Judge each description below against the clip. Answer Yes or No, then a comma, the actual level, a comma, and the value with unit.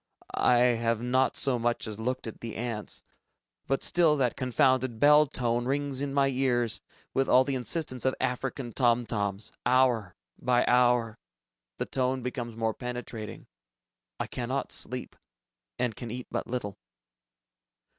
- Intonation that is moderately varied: No, narrow, 2.0 semitones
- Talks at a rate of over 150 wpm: No, average, 145 wpm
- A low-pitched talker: Yes, low, 125 Hz